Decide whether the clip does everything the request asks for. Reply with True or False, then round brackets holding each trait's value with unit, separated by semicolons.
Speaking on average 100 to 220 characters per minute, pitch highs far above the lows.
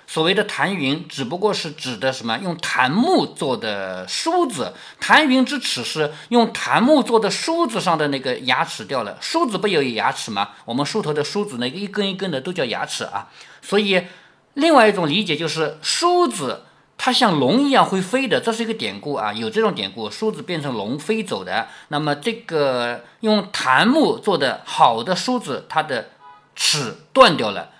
False (270 characters per minute; 7.6 semitones)